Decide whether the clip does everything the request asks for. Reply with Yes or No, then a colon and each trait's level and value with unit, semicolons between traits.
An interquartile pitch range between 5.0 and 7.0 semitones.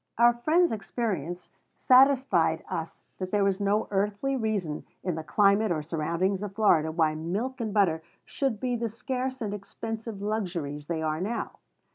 Yes: wide, 5.4 semitones